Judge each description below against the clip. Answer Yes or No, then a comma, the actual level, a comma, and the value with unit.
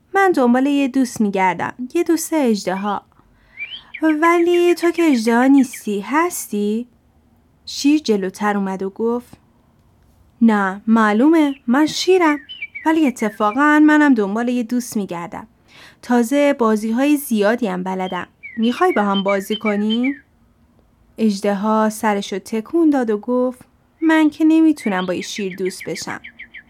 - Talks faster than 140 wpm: No, average, 130 wpm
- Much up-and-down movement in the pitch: Yes, wide, 6.2 semitones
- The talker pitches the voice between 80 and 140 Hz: No, high, 240 Hz